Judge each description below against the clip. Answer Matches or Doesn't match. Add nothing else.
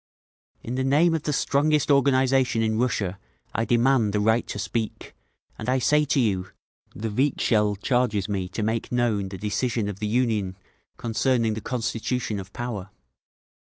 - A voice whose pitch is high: Doesn't match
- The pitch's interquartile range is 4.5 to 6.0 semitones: Doesn't match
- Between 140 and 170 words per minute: Matches